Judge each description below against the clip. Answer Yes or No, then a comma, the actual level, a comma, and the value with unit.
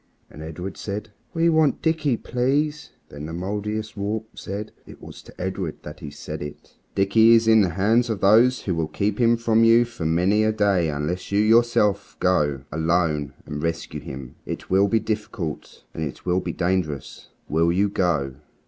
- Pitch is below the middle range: Yes, low, 100 Hz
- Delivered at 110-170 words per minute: No, average, 185 wpm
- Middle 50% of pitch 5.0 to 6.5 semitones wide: Yes, average, 5.3 semitones